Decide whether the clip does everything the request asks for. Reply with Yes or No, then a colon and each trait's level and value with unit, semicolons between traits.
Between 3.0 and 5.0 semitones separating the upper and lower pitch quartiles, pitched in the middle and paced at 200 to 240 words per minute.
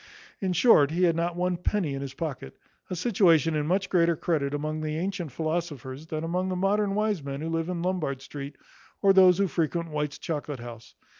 Yes: average, 3.7 semitones; medium, 165 Hz; fast, 205 wpm